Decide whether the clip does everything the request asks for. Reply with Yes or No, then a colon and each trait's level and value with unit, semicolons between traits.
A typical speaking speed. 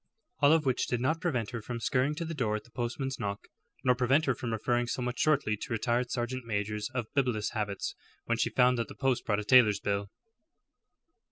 No: fast, 210 wpm